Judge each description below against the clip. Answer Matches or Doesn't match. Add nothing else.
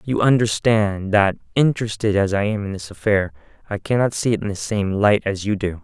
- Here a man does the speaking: Matches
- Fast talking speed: Matches